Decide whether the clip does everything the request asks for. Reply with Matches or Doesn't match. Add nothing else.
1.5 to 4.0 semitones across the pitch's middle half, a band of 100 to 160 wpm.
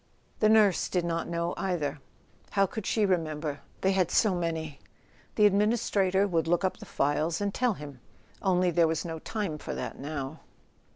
Doesn't match